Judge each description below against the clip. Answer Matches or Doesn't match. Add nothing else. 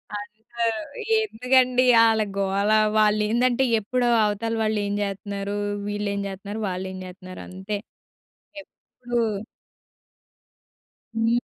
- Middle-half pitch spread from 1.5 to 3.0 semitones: Matches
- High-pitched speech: Matches